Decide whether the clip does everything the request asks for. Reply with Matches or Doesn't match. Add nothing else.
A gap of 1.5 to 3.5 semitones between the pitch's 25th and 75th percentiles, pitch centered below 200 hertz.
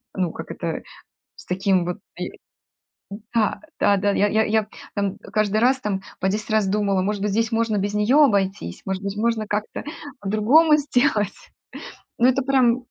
Doesn't match